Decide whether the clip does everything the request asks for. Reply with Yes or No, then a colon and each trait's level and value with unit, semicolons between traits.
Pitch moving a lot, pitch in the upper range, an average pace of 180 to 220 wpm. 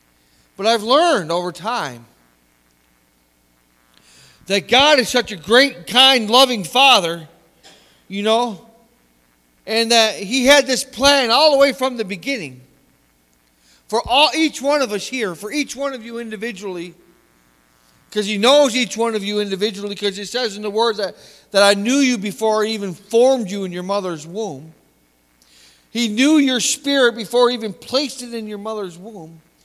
No: wide, 7.4 semitones; high, 210 Hz; average, 165 wpm